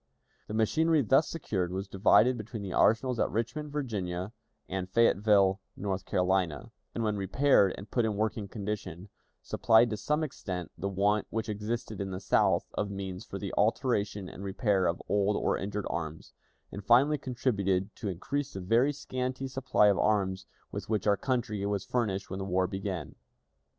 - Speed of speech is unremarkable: Yes, average, 170 wpm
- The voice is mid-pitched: No, low, 105 Hz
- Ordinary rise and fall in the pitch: Yes, average, 3.6 semitones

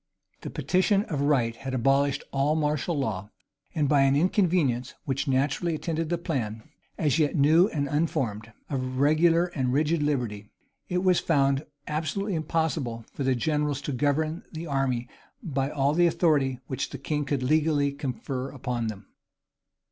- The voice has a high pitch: No, medium, 145 Hz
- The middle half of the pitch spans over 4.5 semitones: No, average, 3.2 semitones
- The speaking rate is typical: Yes, average, 160 wpm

